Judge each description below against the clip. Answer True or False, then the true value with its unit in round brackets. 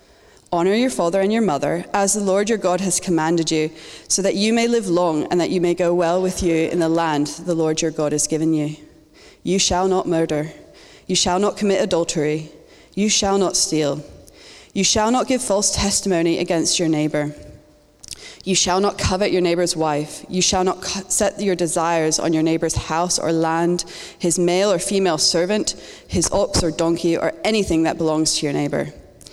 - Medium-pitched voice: True (175 Hz)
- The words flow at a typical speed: True (195 wpm)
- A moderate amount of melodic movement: True (3.2 semitones)